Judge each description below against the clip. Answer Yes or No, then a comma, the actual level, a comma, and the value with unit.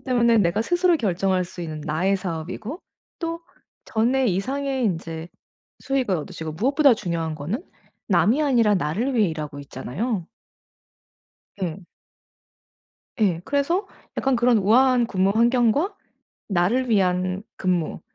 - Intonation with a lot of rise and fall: Yes, wide, 6.6 semitones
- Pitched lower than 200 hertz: No, high, 210 Hz